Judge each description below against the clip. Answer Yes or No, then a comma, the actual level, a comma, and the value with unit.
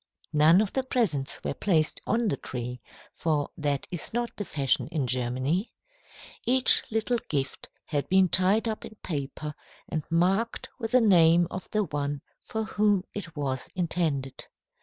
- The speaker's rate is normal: Yes, average, 160 wpm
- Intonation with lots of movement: Yes, wide, 6.8 semitones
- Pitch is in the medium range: Yes, medium, 170 Hz